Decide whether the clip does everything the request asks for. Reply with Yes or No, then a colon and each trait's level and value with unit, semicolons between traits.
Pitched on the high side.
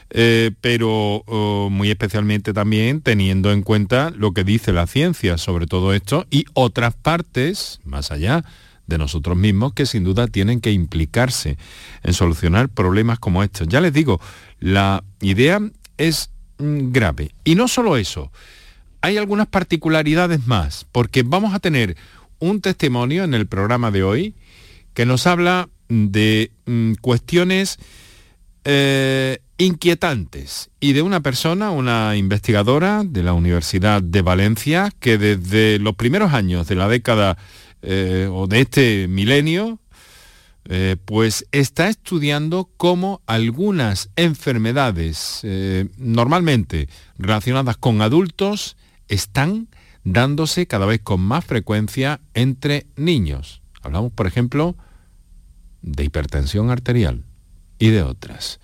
No: low, 110 Hz